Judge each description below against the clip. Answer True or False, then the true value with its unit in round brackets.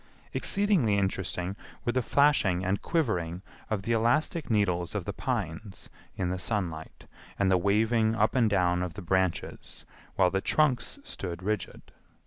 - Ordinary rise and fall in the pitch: True (4.1 semitones)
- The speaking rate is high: False (150 wpm)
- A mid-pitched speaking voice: False (100 Hz)